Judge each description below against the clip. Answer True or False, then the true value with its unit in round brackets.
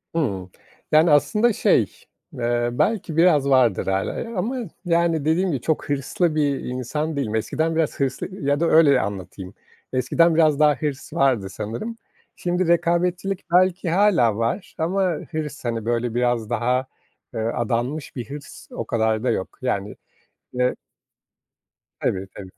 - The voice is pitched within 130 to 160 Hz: True (140 Hz)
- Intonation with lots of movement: True (5.9 semitones)